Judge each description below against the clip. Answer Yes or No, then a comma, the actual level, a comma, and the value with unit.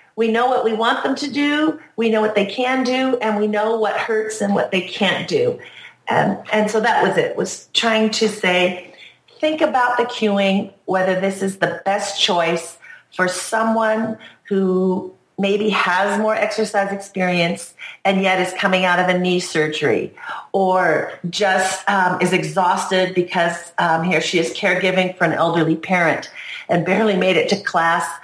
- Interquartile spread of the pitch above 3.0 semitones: Yes, average, 3.4 semitones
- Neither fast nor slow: Yes, average, 175 wpm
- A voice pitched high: Yes, high, 195 Hz